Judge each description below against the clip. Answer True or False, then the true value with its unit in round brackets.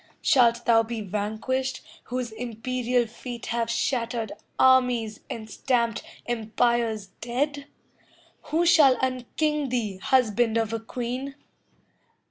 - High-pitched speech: True (240 Hz)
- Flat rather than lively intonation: True (2.3 semitones)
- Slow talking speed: True (105 wpm)